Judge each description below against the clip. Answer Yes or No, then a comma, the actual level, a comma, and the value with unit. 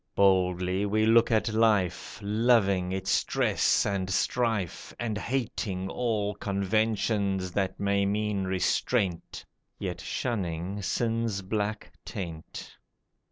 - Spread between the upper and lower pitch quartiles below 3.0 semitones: Yes, narrow, 2.6 semitones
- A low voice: Yes, low, 100 Hz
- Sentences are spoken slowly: Yes, slow, 105 wpm